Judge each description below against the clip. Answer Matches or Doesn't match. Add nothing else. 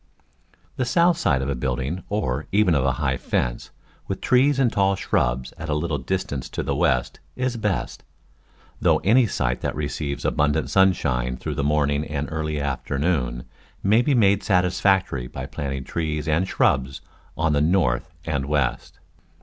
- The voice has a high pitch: Doesn't match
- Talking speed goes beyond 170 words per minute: Doesn't match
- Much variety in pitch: Matches